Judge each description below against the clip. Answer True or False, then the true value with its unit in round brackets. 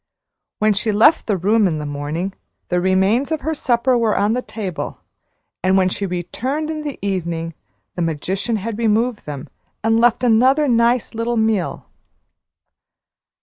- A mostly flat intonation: False (4.5 semitones)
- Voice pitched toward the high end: True (215 Hz)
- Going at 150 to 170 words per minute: True (155 wpm)